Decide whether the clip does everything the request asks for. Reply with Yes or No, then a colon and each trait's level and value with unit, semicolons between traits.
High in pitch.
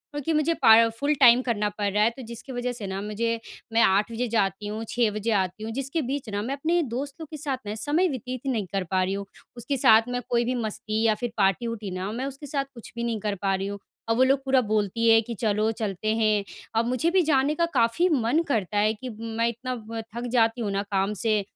Yes: high, 230 Hz